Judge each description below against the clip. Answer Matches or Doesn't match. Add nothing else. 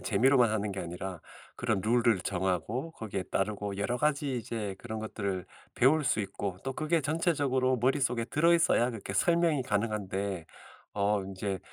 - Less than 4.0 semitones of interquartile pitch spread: Doesn't match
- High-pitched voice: Doesn't match